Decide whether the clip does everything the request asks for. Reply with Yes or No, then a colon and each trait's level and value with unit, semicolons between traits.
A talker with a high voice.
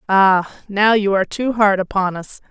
Yes: high, 200 Hz